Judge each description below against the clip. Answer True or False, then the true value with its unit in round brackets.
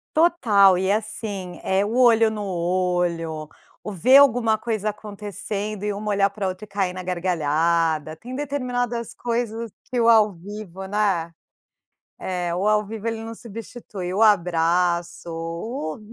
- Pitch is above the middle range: True (200 Hz)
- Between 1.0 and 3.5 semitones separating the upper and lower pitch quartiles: False (4.0 semitones)